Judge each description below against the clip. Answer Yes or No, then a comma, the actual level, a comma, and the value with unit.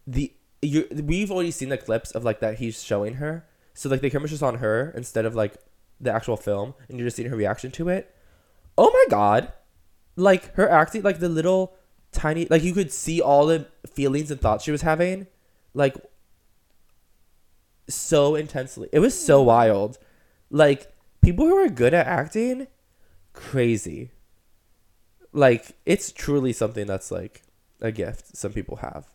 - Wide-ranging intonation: Yes, wide, 7.0 semitones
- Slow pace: No, average, 165 wpm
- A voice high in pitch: No, low, 135 Hz